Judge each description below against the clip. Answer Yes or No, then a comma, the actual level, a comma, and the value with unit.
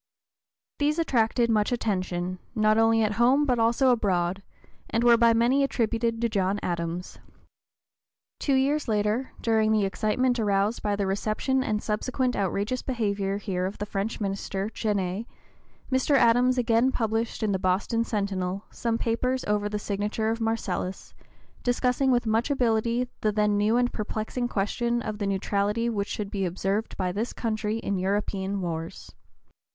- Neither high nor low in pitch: No, high, 215 Hz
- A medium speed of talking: Yes, average, 155 wpm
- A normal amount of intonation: Yes, average, 3.0 semitones